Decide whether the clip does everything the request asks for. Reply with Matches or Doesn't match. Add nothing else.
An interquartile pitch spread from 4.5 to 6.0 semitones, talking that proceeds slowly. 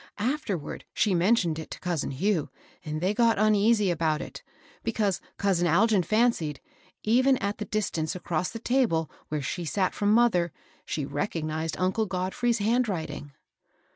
Doesn't match